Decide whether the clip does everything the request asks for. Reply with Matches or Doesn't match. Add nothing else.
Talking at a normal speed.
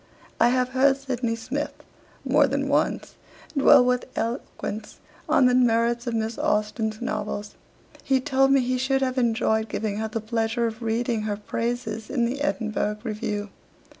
Matches